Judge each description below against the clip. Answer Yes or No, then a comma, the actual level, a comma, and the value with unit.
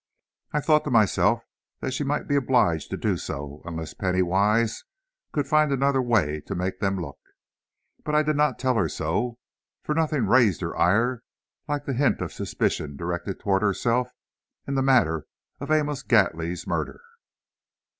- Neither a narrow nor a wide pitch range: No, wide, 7.7 semitones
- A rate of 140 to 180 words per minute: Yes, average, 165 wpm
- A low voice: Yes, low, 115 Hz